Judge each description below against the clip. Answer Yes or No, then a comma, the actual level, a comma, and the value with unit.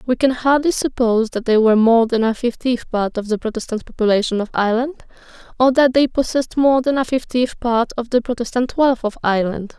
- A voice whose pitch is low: No, high, 240 Hz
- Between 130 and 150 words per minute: No, average, 200 wpm